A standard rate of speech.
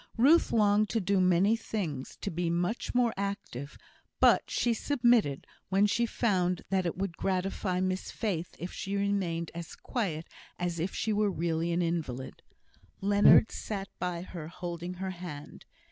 Yes: average, 160 wpm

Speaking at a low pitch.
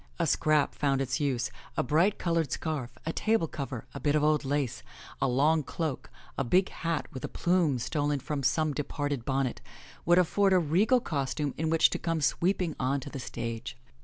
No: medium, 150 Hz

